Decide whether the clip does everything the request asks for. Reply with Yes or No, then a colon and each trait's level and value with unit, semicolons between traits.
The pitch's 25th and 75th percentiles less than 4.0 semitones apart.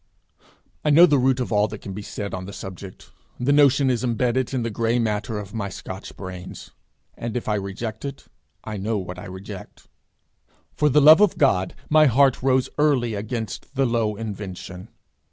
No: average, 4.7 semitones